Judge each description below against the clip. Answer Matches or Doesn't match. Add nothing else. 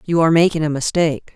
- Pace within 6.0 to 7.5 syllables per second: Matches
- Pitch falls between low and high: Matches